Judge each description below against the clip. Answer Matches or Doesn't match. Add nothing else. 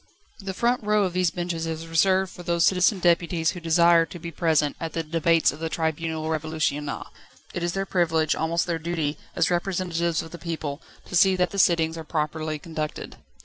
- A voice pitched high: Doesn't match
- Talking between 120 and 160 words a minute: Doesn't match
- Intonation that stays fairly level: Matches